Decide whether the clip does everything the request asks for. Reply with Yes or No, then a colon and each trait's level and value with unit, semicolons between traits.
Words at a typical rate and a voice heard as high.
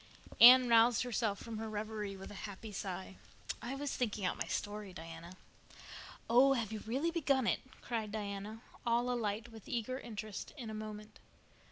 Yes: average, 170 wpm; high, 220 Hz